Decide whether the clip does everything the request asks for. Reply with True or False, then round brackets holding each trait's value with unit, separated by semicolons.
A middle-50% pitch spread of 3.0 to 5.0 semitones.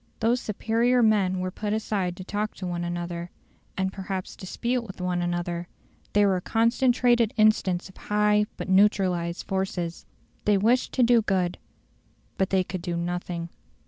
True (3.4 semitones)